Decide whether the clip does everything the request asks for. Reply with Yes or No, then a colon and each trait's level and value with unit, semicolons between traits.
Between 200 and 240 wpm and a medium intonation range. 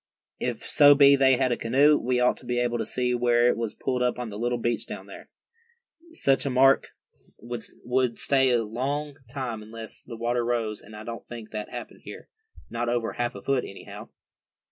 No: fast, 205 wpm; narrow, 2.1 semitones